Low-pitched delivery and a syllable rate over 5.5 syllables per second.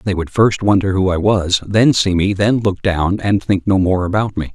No: very low, 95 Hz; 4.8 syllables/s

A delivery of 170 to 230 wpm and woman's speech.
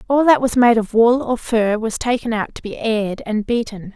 No: fast, 245 wpm; female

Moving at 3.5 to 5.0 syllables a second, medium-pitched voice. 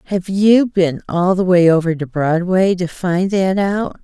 Yes: 4.0 syllables/s; medium, 180 Hz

